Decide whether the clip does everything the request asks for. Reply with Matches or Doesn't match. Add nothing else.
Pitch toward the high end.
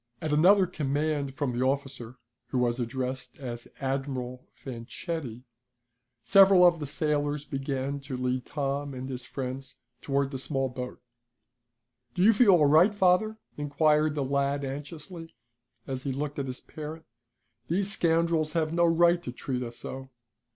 Doesn't match